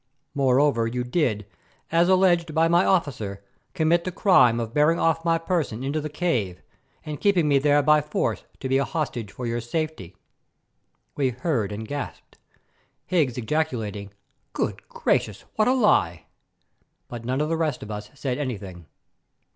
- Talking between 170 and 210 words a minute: No, average, 160 wpm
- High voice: No, medium, 140 Hz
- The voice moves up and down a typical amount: No, wide, 6.0 semitones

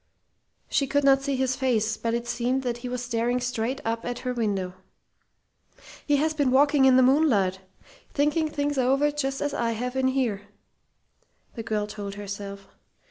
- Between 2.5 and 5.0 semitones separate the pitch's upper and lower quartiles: Yes, average, 3.3 semitones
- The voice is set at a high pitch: Yes, very high, 250 Hz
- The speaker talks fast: No, average, 175 wpm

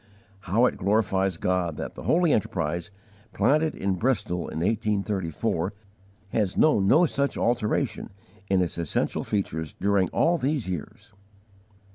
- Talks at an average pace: No, slow, 130 wpm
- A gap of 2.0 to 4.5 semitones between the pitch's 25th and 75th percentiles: No, average, 5.1 semitones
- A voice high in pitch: No, low, 100 Hz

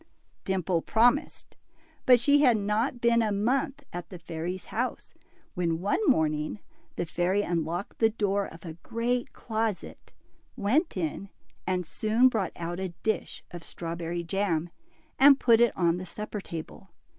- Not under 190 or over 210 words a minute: No, average, 155 wpm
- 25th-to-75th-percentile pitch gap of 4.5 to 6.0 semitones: Yes, average, 5.1 semitones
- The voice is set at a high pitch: Yes, high, 200 Hz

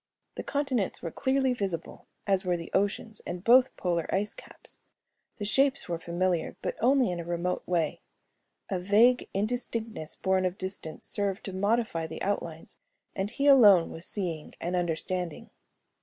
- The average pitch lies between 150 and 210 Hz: Yes, high, 190 Hz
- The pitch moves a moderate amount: Yes, average, 4.6 semitones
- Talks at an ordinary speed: Yes, average, 155 wpm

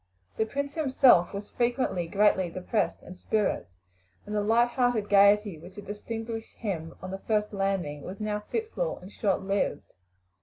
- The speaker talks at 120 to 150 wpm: No, average, 160 wpm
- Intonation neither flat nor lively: Yes, average, 3.2 semitones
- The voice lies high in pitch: Yes, high, 210 Hz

